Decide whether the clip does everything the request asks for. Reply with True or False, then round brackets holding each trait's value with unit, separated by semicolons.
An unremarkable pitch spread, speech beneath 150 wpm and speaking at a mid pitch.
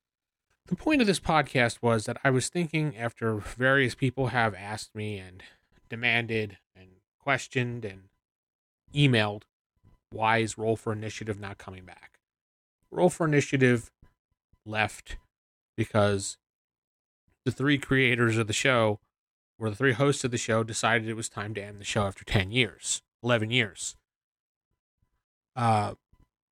False (3.8 semitones; 140 wpm; 110 Hz)